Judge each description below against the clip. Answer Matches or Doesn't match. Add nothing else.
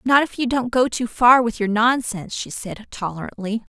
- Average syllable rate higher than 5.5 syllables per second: Doesn't match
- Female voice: Matches